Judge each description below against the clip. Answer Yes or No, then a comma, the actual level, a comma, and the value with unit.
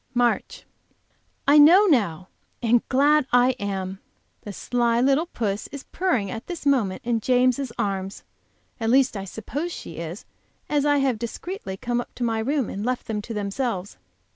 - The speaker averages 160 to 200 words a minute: Yes, average, 165 wpm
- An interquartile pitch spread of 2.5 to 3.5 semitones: No, average, 5.2 semitones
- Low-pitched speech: No, high, 240 Hz